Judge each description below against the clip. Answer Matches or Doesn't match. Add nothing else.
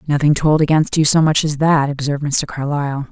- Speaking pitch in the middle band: Matches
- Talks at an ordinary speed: Doesn't match